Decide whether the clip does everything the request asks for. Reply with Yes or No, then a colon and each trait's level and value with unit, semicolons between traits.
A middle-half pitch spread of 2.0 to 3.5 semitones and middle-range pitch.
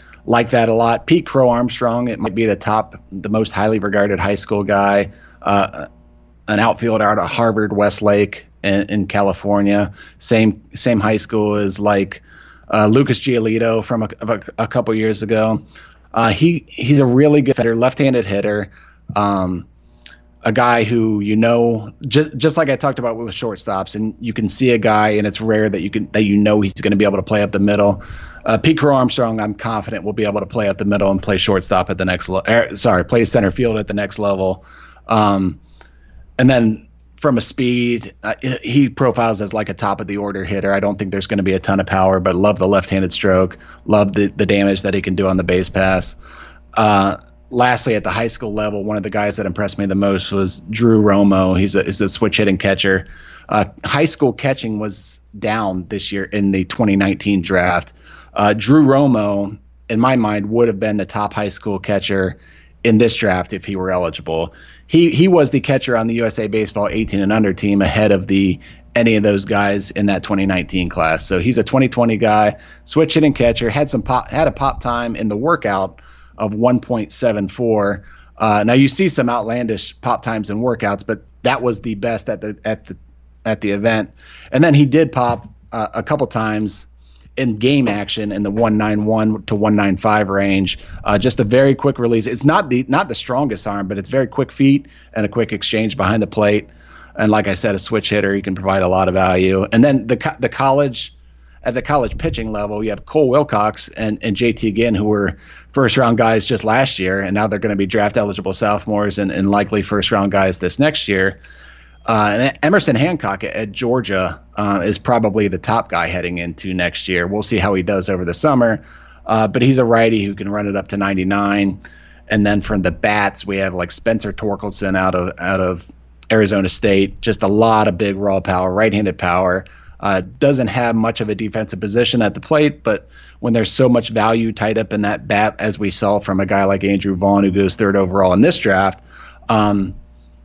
No: average, 2.8 semitones; low, 105 Hz